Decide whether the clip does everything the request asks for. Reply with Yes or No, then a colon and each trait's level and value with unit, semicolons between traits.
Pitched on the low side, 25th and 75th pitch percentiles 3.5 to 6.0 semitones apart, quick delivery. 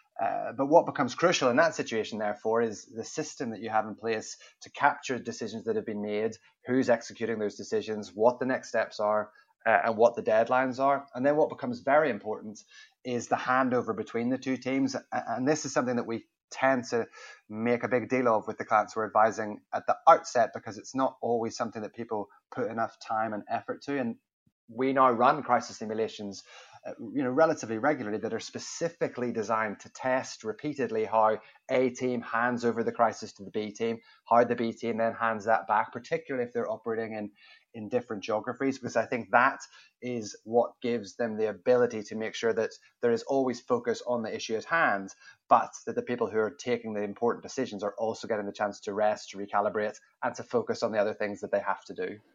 No: low, 115 Hz; average, 2.9 semitones; fast, 210 wpm